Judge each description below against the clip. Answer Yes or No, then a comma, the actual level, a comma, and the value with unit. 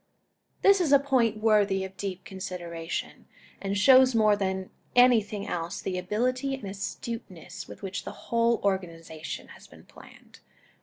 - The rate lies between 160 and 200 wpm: No, average, 145 wpm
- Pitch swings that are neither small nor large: Yes, average, 4.0 semitones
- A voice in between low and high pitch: No, high, 200 Hz